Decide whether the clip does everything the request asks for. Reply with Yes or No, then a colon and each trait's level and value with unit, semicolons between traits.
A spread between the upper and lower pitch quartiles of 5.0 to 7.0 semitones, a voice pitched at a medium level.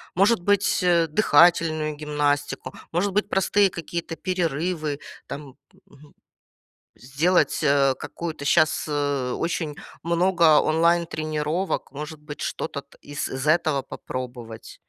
No: average, 3.1 semitones; medium, 155 Hz